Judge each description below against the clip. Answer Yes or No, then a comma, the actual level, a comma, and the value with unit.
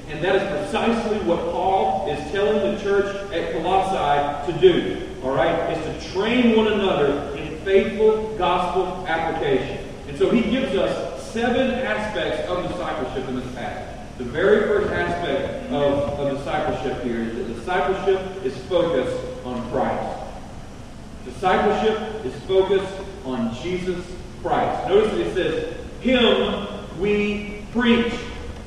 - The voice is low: No, medium, 185 Hz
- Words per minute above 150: No, slow, 135 wpm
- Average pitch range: No, wide, 5.7 semitones